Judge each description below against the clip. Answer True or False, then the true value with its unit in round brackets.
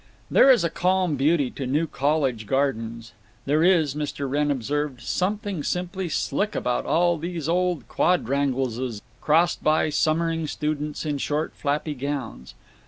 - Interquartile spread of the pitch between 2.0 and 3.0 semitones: False (3.7 semitones)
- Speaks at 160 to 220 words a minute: False (140 wpm)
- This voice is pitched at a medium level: True (150 Hz)